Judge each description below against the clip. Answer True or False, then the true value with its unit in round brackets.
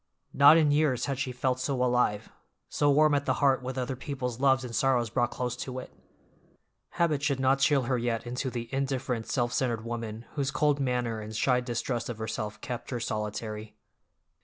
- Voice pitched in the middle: False (125 Hz)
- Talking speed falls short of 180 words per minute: False (190 wpm)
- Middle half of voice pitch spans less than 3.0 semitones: True (2.5 semitones)